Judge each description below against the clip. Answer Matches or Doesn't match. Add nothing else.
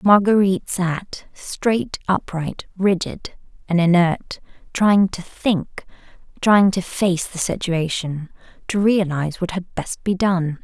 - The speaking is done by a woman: Matches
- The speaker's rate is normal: Doesn't match